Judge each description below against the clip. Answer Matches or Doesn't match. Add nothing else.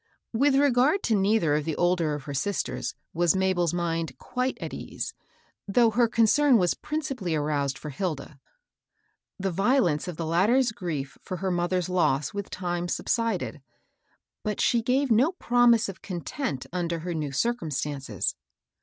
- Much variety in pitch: Matches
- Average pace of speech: Matches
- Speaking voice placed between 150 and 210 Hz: Matches